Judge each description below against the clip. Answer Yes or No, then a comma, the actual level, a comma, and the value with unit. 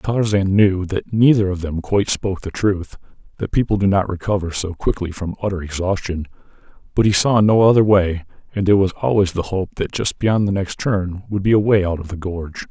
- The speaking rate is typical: No, fast, 215 wpm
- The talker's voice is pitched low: Yes, very low, 95 Hz